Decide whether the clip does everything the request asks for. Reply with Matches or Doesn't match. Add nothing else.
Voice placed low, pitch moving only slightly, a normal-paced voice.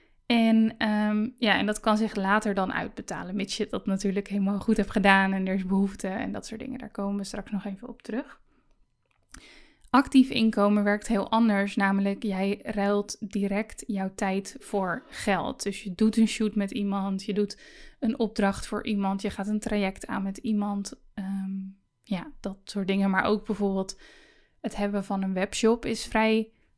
Doesn't match